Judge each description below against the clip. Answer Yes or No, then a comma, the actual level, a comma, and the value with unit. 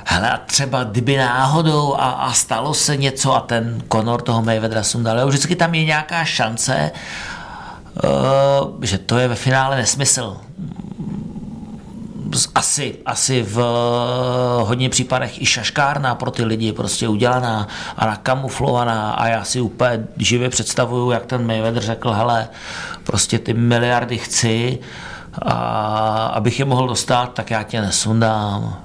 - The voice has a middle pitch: No, low, 120 Hz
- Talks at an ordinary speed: Yes, average, 135 wpm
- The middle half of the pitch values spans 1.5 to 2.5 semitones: No, average, 2.9 semitones